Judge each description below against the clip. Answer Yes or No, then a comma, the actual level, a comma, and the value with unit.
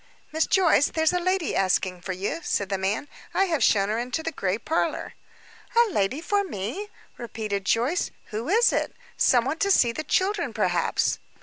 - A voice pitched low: No, very high, 270 Hz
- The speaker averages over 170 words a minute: Yes, average, 185 wpm